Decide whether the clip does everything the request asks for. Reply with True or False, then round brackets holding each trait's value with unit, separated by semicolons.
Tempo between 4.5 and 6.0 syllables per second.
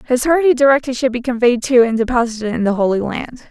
False (6.3 syllables/s)